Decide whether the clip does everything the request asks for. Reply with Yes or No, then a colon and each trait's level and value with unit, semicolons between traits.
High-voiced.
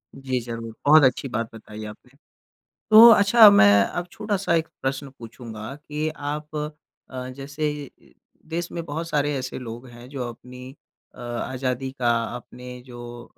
No: low, 130 Hz